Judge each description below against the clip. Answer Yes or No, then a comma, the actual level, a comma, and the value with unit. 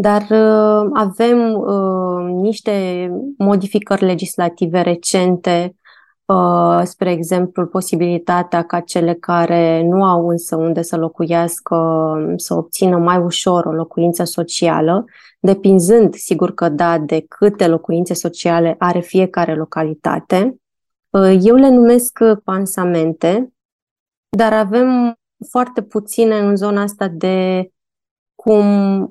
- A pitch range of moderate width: Yes, average, 3.3 semitones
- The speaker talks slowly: Yes, slow, 110 wpm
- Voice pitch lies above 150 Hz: Yes, medium, 185 Hz